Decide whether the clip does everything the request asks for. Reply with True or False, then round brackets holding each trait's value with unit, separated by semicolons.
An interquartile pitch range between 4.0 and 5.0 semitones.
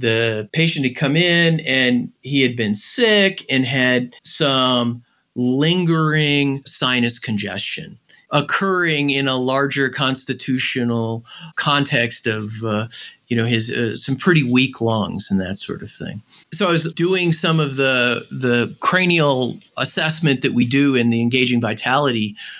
True (4.6 semitones)